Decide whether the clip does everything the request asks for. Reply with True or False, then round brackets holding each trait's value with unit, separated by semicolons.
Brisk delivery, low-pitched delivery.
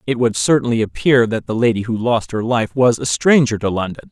True (235 wpm; 120 Hz)